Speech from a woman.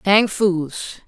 Yes: female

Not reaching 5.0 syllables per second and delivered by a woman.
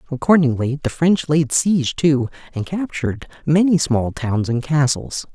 No: 4.6 syllables/s; male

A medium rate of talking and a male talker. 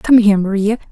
No: average, 195 wpm; female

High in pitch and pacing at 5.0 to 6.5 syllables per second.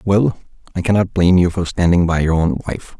No: very low, 90 Hz; 5.8 syllables/s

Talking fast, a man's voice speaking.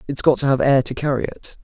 Yes: fast, 295 wpm; male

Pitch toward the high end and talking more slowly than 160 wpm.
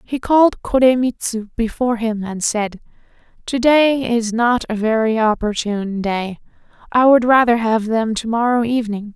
Yes: high, 230 Hz; average, 150 wpm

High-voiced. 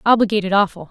Yes: high, 200 Hz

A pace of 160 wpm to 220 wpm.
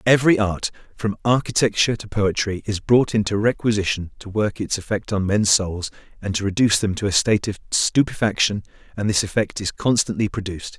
Yes: average, 180 wpm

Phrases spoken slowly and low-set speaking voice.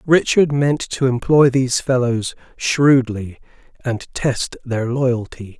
Yes: slow, 120 wpm; low, 125 Hz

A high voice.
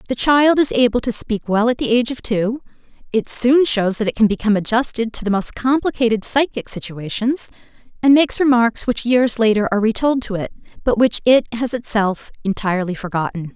Yes: high, 230 Hz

